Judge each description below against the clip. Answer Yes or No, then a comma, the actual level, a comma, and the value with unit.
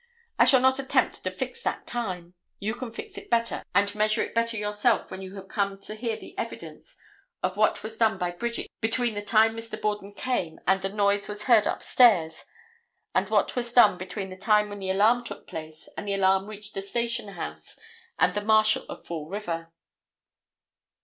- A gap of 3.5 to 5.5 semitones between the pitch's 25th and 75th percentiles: No, average, 3.1 semitones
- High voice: Yes, high, 210 Hz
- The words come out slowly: No, average, 195 wpm